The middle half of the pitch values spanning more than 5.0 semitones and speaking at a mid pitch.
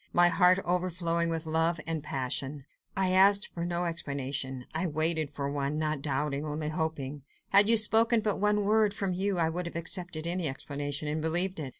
No: average, 3.8 semitones; medium, 165 Hz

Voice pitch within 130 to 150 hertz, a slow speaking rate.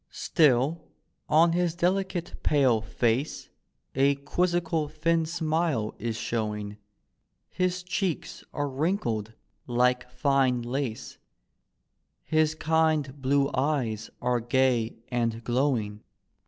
Yes: medium, 140 Hz; slow, 100 wpm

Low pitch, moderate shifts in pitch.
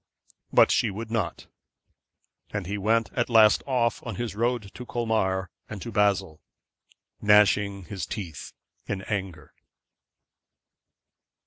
Yes: low, 105 Hz; average, 3.0 semitones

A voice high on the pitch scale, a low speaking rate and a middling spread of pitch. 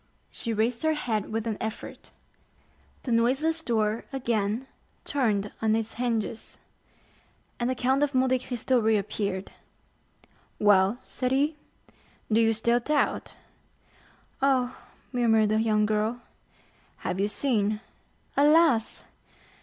Yes: high, 230 Hz; slow, 115 wpm; average, 3.2 semitones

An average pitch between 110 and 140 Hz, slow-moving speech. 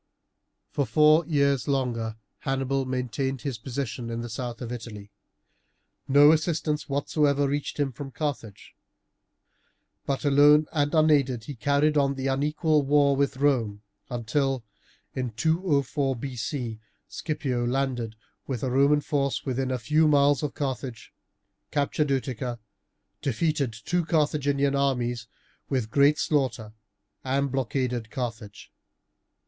Yes: low, 135 Hz; slow, 120 wpm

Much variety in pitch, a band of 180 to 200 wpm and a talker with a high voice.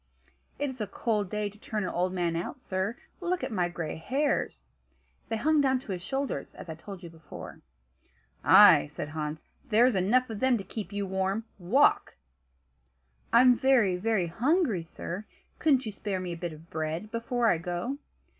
Yes: wide, 5.9 semitones; average, 190 wpm; high, 205 Hz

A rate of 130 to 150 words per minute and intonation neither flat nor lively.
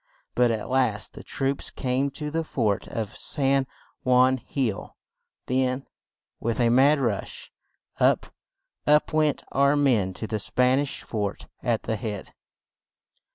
Yes: average, 140 wpm; average, 3.7 semitones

